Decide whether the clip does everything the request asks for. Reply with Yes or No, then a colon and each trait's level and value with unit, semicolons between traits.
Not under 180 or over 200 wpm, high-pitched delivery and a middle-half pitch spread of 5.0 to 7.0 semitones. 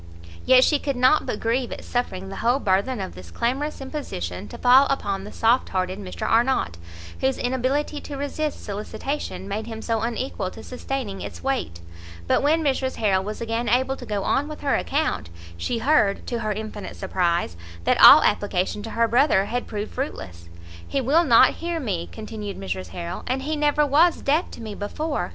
Yes: average, 190 wpm; high, 235 Hz; wide, 5.5 semitones